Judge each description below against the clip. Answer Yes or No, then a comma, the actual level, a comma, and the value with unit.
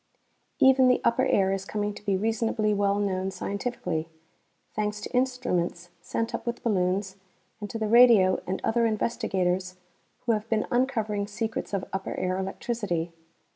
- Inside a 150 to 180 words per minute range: Yes, average, 155 wpm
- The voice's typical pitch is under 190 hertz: No, high, 210 Hz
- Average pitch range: Yes, average, 3.4 semitones